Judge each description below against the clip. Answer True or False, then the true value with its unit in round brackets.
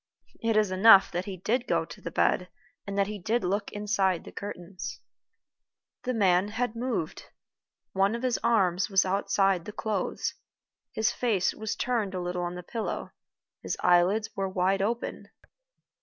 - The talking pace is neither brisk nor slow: True (165 wpm)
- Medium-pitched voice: False (200 Hz)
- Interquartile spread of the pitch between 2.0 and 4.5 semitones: True (2.9 semitones)